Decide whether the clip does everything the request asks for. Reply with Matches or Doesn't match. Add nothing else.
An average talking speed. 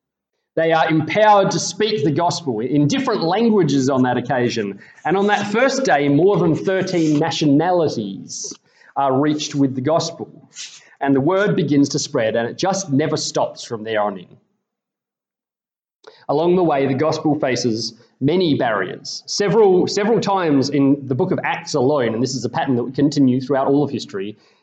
Matches